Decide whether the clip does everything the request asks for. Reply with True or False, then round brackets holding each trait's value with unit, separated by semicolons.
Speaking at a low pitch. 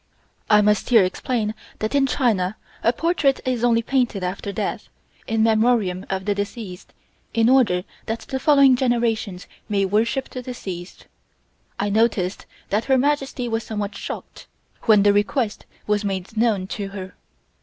False (220 Hz)